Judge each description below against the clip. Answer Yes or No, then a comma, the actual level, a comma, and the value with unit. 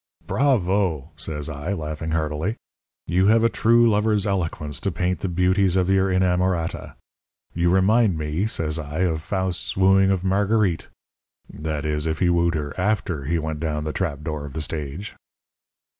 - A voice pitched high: No, very low, 90 Hz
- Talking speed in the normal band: Yes, average, 165 wpm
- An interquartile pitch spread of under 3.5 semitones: No, average, 3.8 semitones